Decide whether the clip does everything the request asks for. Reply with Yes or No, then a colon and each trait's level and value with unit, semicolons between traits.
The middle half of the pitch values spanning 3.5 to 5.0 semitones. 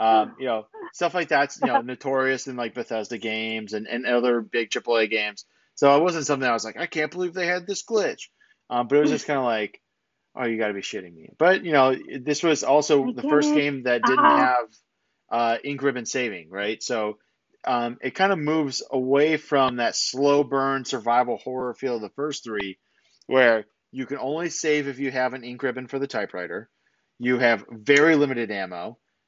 Yes: average, 4.0 semitones